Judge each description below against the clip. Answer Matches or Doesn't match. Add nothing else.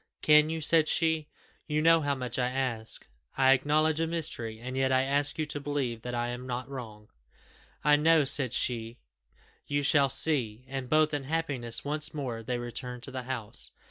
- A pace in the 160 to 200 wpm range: Matches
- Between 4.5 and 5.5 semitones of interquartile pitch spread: Doesn't match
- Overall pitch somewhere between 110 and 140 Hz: Matches